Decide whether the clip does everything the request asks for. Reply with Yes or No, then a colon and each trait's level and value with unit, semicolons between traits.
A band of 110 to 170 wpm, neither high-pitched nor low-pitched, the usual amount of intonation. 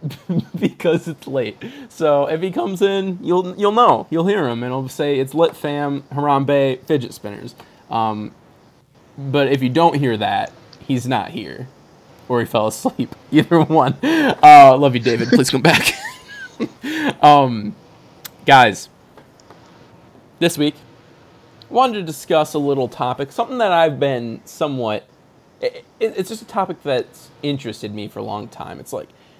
No: average, 155 wpm; medium, 150 Hz; wide, 6.4 semitones